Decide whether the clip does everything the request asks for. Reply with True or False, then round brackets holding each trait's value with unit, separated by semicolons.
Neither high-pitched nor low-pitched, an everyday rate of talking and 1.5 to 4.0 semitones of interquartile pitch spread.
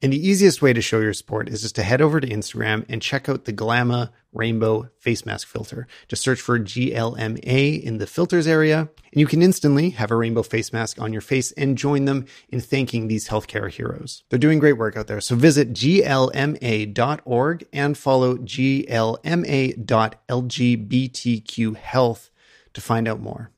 False (120 Hz; 175 wpm; 3.7 semitones)